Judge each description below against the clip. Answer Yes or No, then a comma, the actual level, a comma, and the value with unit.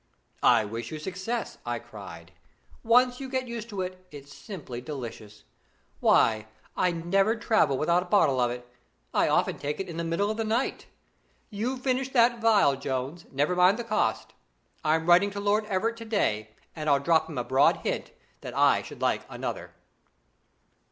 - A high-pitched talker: No, medium, 175 Hz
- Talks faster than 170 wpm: Yes, average, 180 wpm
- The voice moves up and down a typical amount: No, wide, 8.3 semitones